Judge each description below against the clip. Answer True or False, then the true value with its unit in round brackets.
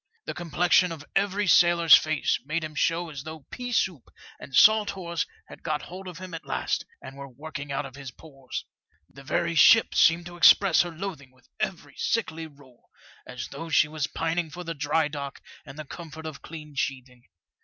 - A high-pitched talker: False (160 Hz)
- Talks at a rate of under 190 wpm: False (195 wpm)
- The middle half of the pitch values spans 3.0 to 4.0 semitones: True (3.5 semitones)